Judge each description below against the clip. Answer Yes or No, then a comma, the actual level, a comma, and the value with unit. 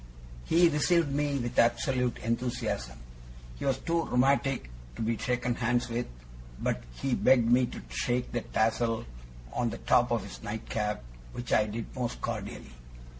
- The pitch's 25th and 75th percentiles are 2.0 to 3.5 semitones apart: Yes, narrow, 2.6 semitones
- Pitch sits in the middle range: No, low, 120 Hz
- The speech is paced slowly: No, average, 155 wpm